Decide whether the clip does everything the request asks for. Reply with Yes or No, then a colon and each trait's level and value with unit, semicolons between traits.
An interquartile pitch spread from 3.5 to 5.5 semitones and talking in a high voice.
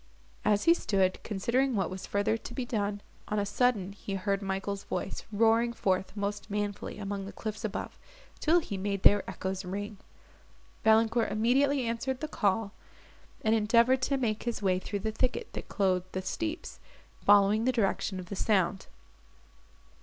No: average, 3.0 semitones; high, 210 Hz